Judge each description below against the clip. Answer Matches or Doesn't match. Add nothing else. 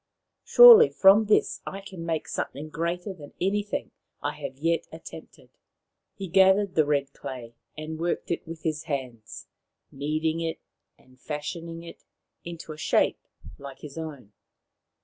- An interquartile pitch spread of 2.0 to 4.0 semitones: Matches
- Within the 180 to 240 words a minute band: Doesn't match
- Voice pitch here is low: Doesn't match